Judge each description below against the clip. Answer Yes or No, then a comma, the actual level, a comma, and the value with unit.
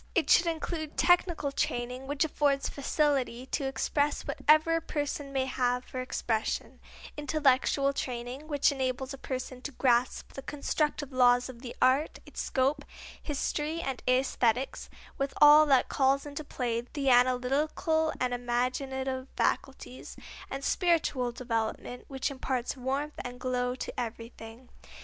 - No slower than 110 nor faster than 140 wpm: Yes, slow, 135 wpm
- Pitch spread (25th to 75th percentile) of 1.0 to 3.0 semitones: Yes, average, 2.7 semitones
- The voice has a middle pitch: No, very high, 265 Hz